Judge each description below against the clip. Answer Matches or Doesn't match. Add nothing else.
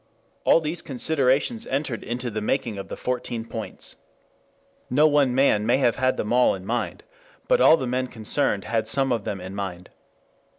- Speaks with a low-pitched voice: Matches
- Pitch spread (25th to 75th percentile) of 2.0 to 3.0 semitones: Doesn't match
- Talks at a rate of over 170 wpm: Matches